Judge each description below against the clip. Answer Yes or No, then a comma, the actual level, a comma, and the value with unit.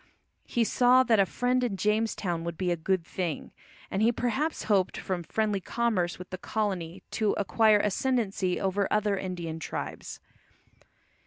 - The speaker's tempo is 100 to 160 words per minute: Yes, average, 155 wpm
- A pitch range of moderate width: Yes, average, 3.6 semitones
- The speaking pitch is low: No, high, 200 Hz